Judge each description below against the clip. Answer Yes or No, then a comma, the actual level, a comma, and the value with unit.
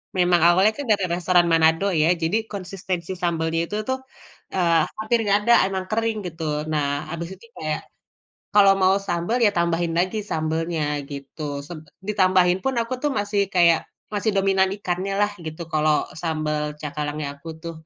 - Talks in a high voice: No, medium, 175 Hz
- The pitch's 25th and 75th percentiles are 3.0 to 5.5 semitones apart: Yes, average, 3.7 semitones